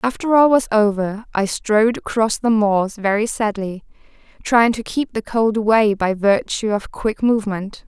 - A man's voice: No, female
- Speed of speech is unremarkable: Yes, average, 170 wpm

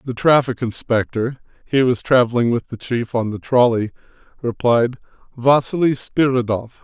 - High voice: No, low, 120 Hz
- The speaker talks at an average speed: No, slow, 130 wpm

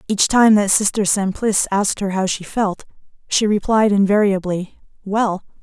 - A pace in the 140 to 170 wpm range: Yes, average, 150 wpm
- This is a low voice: No, high, 200 Hz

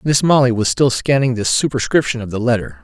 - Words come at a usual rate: No, fast, 210 wpm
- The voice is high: No, low, 120 Hz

